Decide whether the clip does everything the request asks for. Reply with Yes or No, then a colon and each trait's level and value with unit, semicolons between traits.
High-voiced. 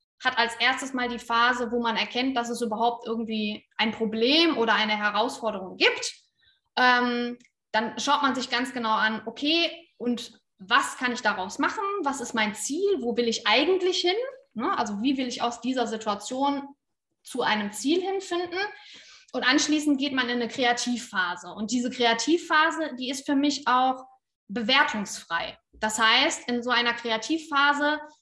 Yes: high, 245 Hz